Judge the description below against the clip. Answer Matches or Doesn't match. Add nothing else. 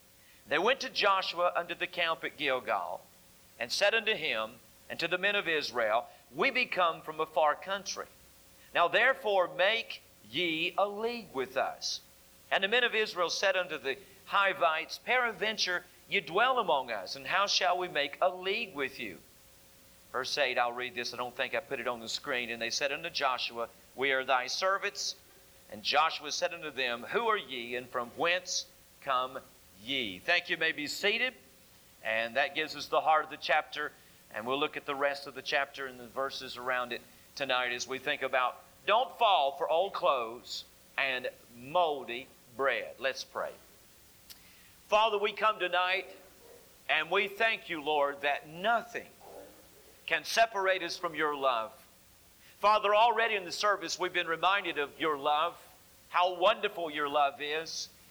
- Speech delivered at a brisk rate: Doesn't match